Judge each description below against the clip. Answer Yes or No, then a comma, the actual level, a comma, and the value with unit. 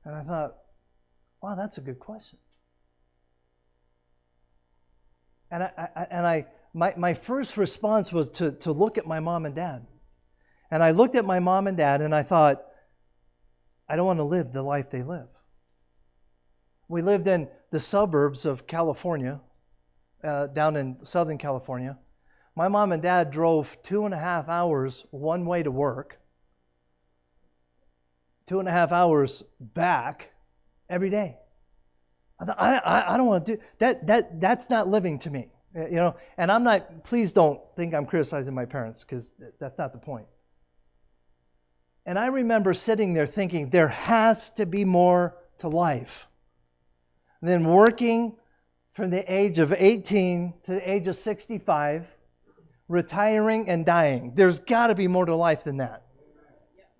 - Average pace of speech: Yes, average, 155 wpm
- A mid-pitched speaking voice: Yes, medium, 155 Hz